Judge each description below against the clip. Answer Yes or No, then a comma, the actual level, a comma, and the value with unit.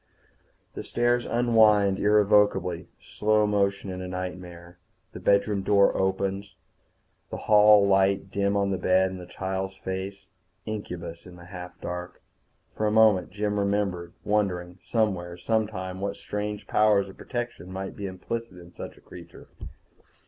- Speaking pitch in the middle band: No, low, 100 Hz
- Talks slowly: No, average, 145 wpm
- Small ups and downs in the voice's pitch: Yes, narrow, 2.2 semitones